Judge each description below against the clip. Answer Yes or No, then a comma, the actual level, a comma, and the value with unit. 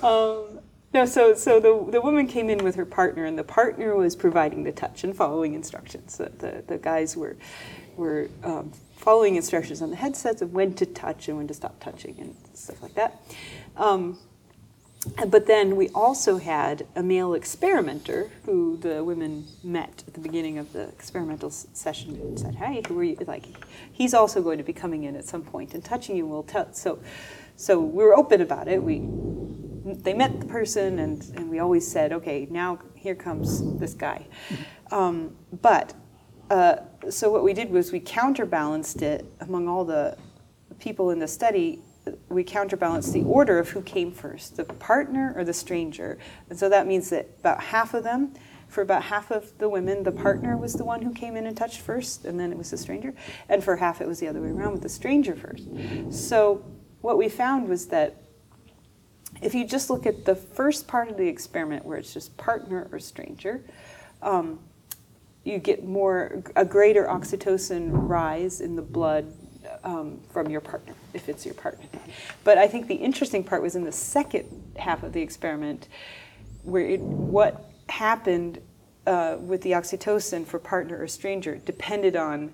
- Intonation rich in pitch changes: Yes, wide, 6.1 semitones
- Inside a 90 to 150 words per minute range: No, average, 190 wpm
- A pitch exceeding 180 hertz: Yes, high, 190 Hz